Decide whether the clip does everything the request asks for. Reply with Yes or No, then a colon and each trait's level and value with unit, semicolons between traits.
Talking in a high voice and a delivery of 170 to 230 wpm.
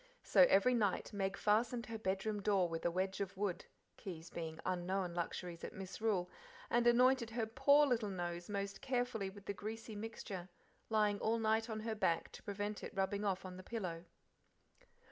Yes: high, 205 Hz; average, 180 wpm